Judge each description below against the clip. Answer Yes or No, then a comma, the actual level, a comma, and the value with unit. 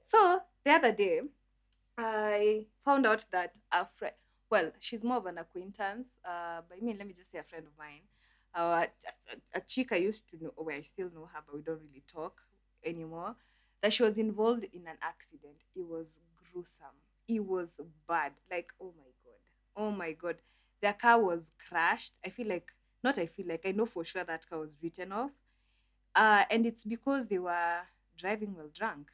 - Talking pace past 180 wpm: Yes, average, 200 wpm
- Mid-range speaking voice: Yes, medium, 180 Hz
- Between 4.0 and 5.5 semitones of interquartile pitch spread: Yes, average, 5.1 semitones